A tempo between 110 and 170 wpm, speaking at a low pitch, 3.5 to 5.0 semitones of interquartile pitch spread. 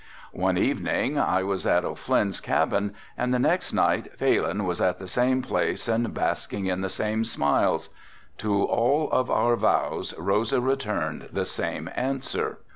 Yes: average, 155 wpm; low, 105 Hz; average, 4.5 semitones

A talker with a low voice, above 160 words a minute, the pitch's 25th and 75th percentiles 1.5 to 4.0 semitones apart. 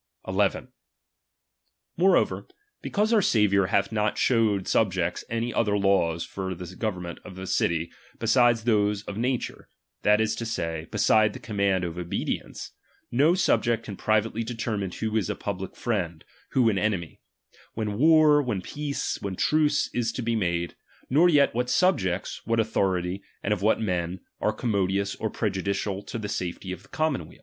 Yes: low, 105 Hz; average, 175 wpm; average, 3.7 semitones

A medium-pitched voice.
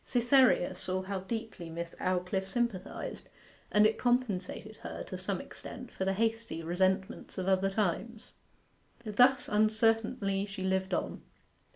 No: high, 195 Hz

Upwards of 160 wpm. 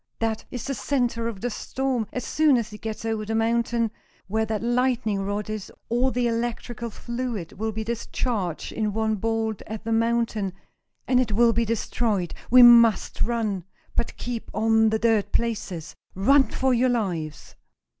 Yes: average, 170 wpm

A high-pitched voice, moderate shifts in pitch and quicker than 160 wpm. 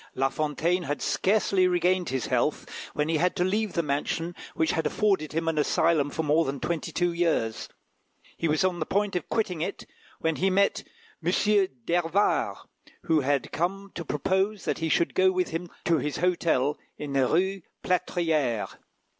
No: medium, 170 Hz; average, 3.4 semitones; average, 180 wpm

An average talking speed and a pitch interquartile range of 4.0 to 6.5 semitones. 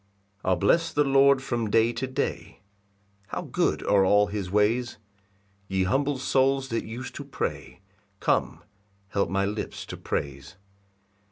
Yes: average, 150 wpm; average, 5.1 semitones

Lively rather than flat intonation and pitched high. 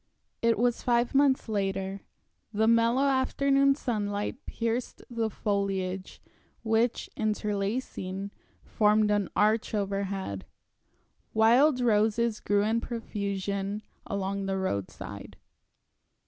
No: average, 2.8 semitones; high, 215 Hz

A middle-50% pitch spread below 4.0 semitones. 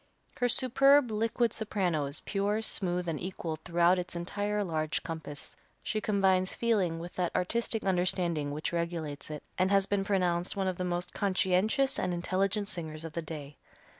Yes: average, 3.3 semitones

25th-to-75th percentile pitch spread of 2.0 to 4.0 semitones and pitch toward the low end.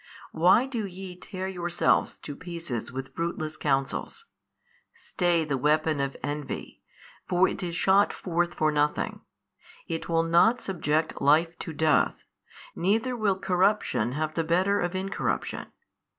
No: average, 3.5 semitones; medium, 170 Hz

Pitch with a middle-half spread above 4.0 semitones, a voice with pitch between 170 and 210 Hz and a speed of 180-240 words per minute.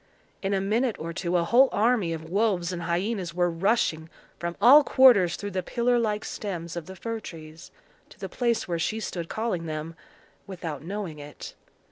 Yes: average, 4.7 semitones; medium, 185 Hz; average, 185 wpm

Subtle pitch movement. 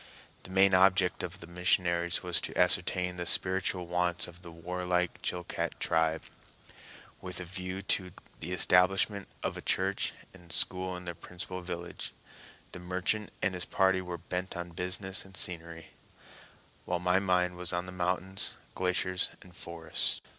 Yes: narrow, 0.9 semitones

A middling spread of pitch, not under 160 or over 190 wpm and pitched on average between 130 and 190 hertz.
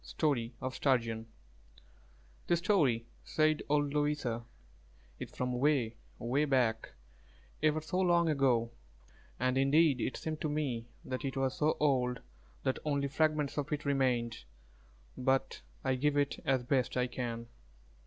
No: average, 3.2 semitones; average, 140 wpm; low, 135 Hz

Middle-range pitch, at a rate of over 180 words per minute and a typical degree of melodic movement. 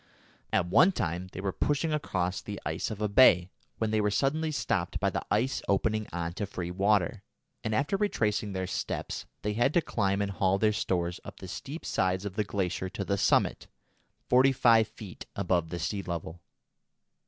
No: low, 100 Hz; average, 190 wpm; average, 3.5 semitones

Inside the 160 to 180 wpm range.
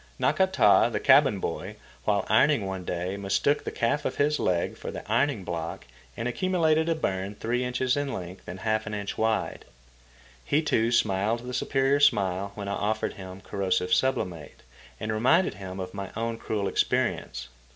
Yes: average, 170 wpm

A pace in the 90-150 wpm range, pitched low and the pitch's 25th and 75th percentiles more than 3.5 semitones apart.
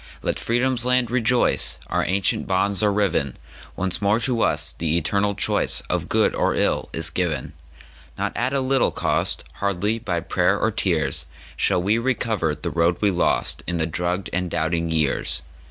Yes: average, 145 wpm; low, 100 Hz; average, 5.3 semitones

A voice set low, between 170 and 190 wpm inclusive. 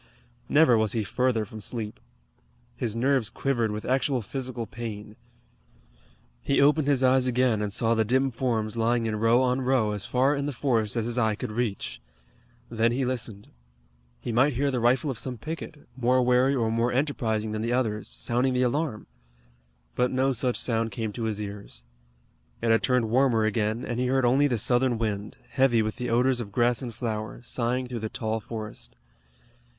Yes: low, 120 Hz; average, 185 wpm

